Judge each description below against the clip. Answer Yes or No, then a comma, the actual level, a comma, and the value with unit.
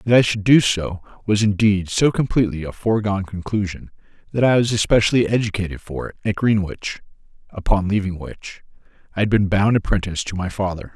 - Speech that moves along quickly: No, average, 175 wpm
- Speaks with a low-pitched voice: Yes, low, 100 Hz